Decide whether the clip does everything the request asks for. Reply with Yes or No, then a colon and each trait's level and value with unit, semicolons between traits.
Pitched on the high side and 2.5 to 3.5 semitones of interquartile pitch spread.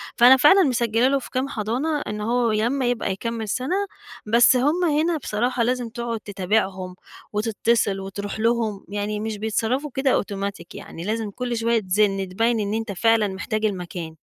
Yes: high, 225 Hz; average, 3.2 semitones